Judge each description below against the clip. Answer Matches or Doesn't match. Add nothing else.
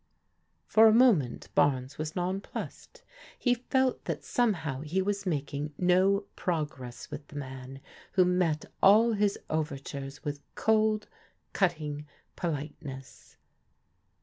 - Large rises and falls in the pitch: Matches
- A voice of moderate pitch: Matches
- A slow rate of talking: Matches